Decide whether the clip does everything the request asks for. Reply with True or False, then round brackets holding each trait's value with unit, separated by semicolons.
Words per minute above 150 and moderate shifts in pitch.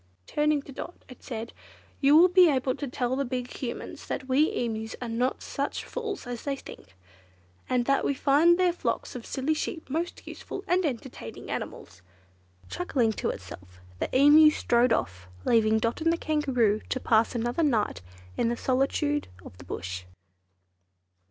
True (170 wpm; 4.7 semitones)